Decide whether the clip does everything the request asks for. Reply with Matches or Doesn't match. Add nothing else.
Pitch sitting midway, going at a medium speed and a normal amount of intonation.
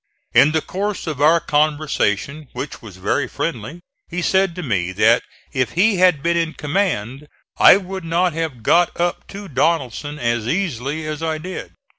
Matches